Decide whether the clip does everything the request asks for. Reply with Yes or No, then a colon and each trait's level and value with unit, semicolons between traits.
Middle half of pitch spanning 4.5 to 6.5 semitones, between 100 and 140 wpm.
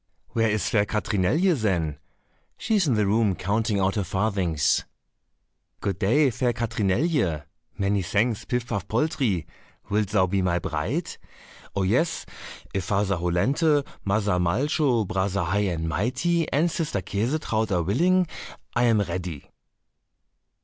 Yes: average, 4.9 semitones; slow, 135 wpm